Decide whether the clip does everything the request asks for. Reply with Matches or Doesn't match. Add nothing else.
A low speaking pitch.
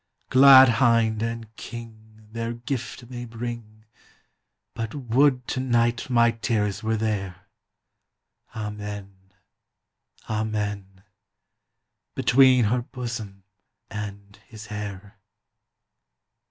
Matches